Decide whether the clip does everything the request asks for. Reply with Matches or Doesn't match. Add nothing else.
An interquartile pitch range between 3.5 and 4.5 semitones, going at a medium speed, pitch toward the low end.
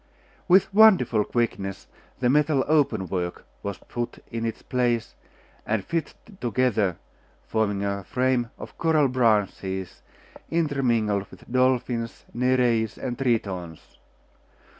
Doesn't match